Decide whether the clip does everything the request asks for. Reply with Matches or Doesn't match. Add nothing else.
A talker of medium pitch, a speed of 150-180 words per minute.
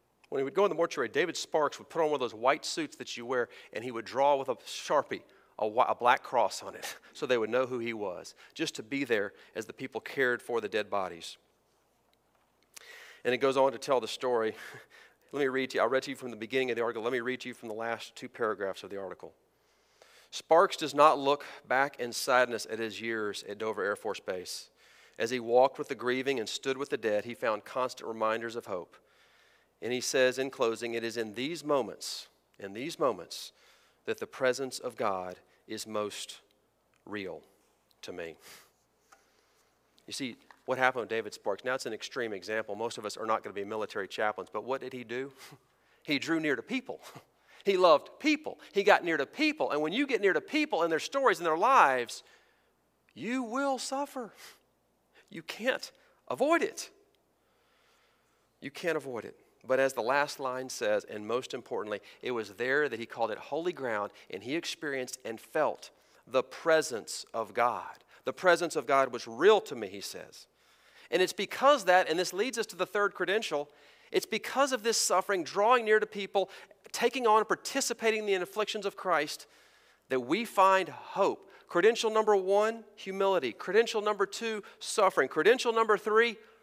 Doesn't match